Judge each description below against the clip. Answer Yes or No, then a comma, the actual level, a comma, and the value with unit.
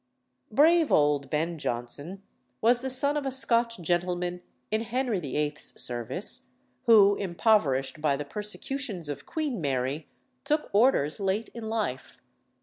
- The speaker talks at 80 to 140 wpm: Yes, slow, 135 wpm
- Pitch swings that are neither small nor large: No, wide, 8.1 semitones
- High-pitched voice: Yes, high, 195 Hz